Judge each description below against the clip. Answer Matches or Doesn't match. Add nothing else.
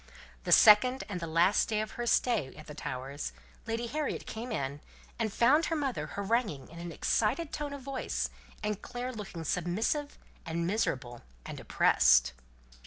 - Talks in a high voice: Matches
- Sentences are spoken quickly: Doesn't match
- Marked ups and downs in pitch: Matches